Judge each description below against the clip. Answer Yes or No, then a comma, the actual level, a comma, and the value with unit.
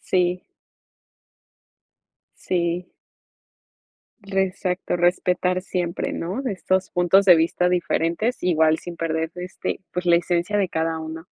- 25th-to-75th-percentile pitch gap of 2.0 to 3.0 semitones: No, narrow, 1.5 semitones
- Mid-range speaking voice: Yes, medium, 180 Hz